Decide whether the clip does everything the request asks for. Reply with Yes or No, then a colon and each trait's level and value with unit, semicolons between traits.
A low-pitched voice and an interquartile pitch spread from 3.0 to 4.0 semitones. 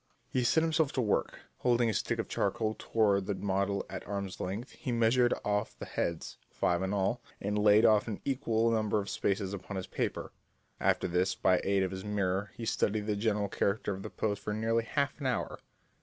No: low, 105 Hz; narrow, 2.6 semitones